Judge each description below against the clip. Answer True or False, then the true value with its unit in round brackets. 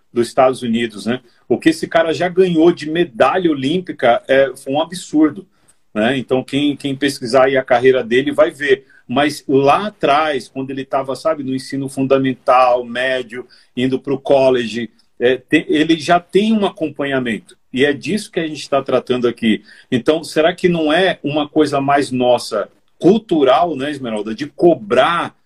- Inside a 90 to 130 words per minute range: False (170 wpm)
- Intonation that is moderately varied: True (4.0 semitones)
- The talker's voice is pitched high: False (135 Hz)